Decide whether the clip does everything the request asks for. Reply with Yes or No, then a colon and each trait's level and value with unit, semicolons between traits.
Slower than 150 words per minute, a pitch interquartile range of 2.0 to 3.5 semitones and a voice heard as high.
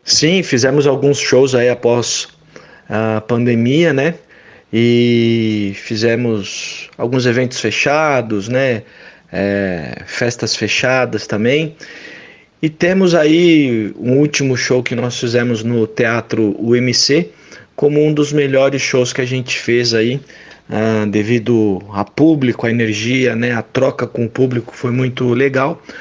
No: average, 130 wpm; average, 3.0 semitones; low, 125 Hz